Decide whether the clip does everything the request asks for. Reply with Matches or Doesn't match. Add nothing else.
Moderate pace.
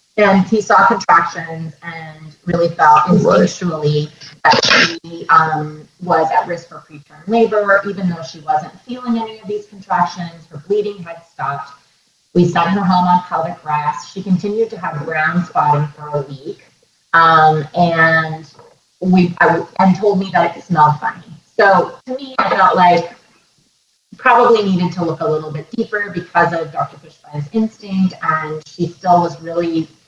Matches